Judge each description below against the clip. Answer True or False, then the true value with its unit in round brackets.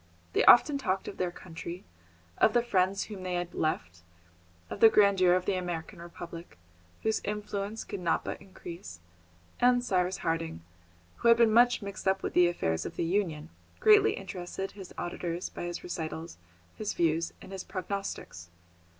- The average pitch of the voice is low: False (185 Hz)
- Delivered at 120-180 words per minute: True (165 wpm)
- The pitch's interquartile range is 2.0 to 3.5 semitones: True (3.1 semitones)